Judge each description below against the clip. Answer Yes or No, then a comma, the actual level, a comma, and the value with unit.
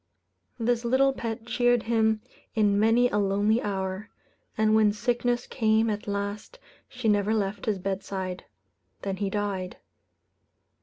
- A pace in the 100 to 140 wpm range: Yes, slow, 135 wpm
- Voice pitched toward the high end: Yes, high, 215 Hz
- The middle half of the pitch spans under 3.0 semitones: Yes, narrow, 2.5 semitones